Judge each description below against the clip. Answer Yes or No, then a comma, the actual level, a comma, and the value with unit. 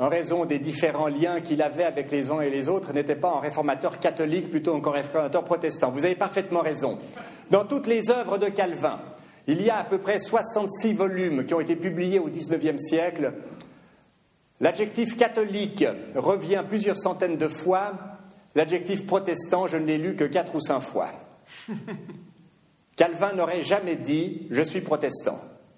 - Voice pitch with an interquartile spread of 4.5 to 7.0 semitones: No, average, 3.8 semitones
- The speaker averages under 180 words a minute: Yes, average, 170 wpm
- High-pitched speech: No, medium, 175 Hz